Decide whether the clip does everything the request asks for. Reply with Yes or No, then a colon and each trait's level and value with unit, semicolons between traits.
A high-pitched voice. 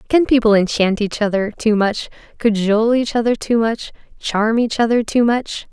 Yes: high, 225 Hz